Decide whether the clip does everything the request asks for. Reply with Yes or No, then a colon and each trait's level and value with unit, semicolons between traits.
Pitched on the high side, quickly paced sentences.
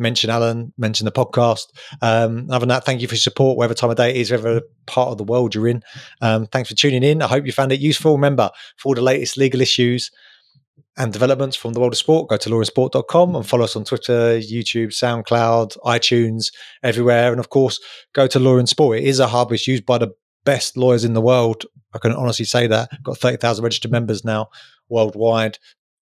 No: low, 120 Hz; fast, 225 wpm